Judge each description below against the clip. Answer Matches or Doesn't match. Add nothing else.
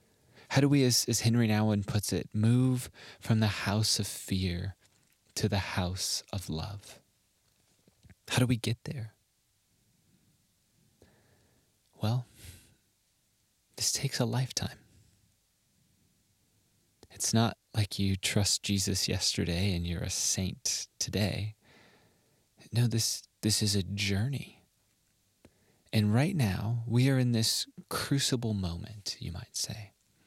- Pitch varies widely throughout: Doesn't match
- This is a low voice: Matches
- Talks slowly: Matches